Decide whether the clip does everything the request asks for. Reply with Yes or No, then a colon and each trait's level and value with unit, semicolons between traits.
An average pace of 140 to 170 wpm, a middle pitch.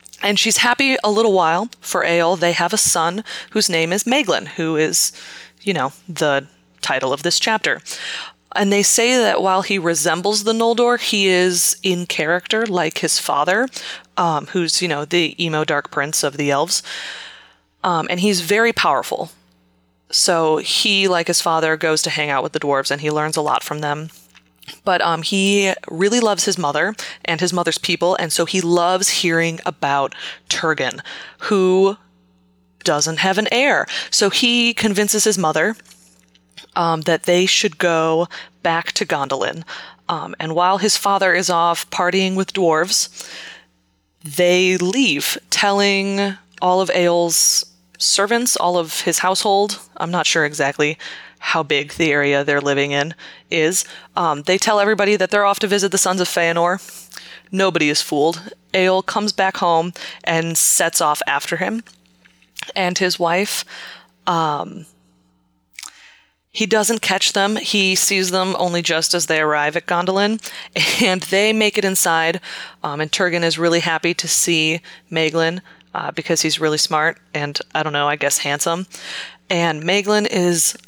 Yes: average, 160 wpm; medium, 175 Hz